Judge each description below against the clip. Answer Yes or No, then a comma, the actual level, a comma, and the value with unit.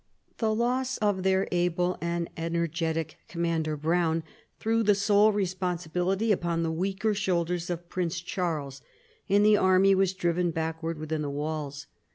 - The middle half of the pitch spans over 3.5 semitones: No, average, 3.0 semitones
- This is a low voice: No, medium, 175 Hz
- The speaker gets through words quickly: No, average, 150 wpm